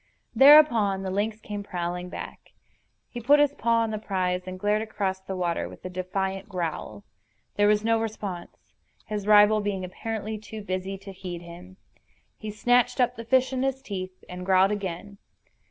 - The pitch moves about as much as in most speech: Yes, average, 3.1 semitones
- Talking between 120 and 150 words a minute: No, average, 175 wpm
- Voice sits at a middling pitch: No, high, 205 Hz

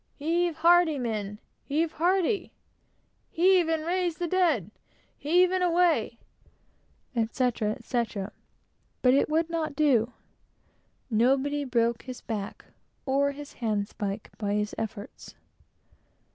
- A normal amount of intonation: No, wide, 6.8 semitones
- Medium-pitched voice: No, very high, 280 Hz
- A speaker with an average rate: No, slow, 115 wpm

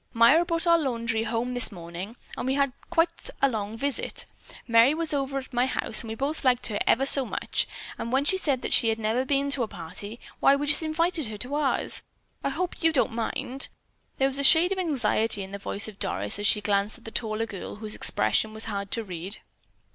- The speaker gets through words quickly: Yes, fast, 230 wpm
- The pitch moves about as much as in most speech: Yes, average, 4.6 semitones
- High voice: Yes, high, 245 Hz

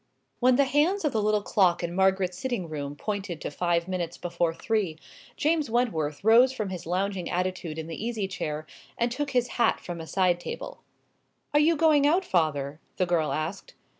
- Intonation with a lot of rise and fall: Yes, wide, 6.1 semitones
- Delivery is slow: No, average, 190 wpm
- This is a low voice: No, high, 190 Hz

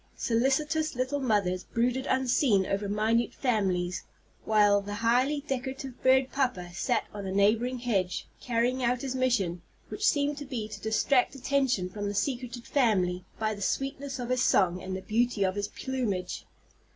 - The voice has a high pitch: Yes, high, 235 Hz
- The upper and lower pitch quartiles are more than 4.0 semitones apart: Yes, average, 4.5 semitones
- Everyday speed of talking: Yes, average, 165 wpm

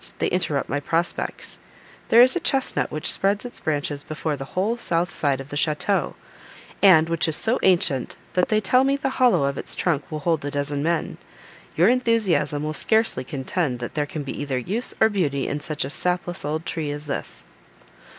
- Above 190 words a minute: Yes, average, 200 wpm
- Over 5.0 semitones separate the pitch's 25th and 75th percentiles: Yes, wide, 5.6 semitones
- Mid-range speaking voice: Yes, medium, 160 Hz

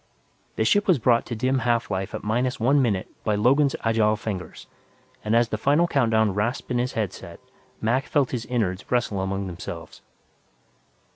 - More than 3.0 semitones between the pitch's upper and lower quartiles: Yes, average, 3.5 semitones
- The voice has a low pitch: Yes, low, 115 Hz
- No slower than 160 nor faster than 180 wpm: Yes, average, 170 wpm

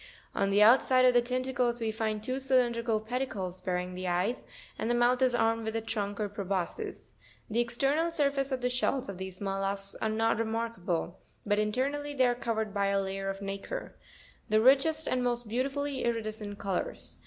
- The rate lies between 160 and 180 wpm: No, average, 190 wpm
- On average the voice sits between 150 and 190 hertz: No, high, 225 Hz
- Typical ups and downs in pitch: Yes, average, 4.2 semitones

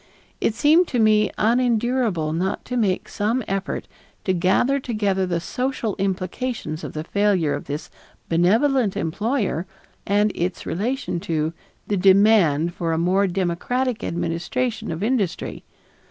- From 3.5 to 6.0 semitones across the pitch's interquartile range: Yes, average, 5.3 semitones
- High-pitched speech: Yes, high, 200 Hz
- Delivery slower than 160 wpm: Yes, slow, 135 wpm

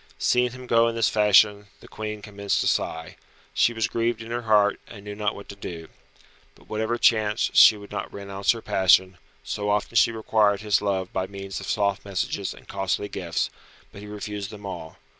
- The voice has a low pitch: Yes, low, 105 Hz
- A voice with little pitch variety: Yes, narrow, 1.8 semitones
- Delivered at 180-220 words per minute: Yes, average, 200 wpm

